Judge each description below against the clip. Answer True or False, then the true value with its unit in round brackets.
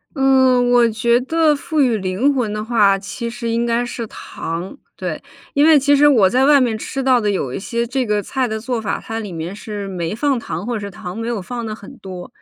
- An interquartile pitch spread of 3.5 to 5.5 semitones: True (3.9 semitones)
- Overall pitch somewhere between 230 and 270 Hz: True (235 Hz)